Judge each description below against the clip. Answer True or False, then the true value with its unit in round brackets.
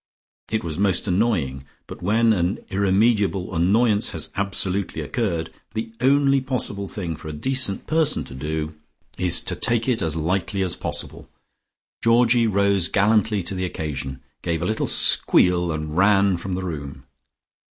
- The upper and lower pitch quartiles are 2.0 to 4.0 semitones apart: False (4.9 semitones)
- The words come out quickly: False (150 wpm)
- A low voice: True (95 Hz)